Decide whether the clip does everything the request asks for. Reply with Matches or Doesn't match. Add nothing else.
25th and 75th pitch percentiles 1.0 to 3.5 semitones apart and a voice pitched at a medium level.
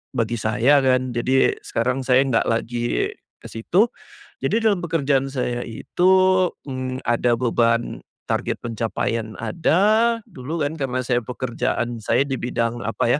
Doesn't match